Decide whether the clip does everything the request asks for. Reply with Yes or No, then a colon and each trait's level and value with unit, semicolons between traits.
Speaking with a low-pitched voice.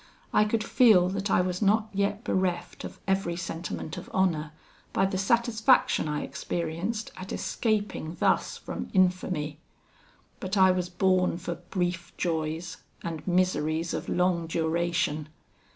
No: medium, 180 Hz